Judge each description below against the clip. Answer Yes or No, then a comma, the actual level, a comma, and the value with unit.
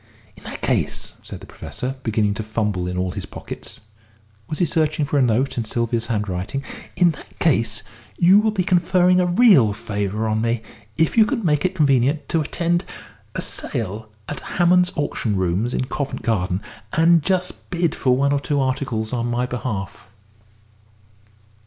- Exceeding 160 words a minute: Yes, average, 170 wpm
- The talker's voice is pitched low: Yes, low, 130 Hz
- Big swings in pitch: Yes, wide, 7.4 semitones